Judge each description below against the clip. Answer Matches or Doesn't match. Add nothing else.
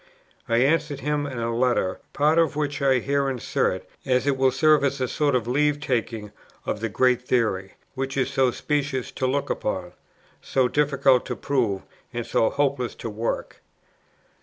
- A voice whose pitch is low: Matches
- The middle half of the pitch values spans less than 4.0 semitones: Matches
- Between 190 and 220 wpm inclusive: Doesn't match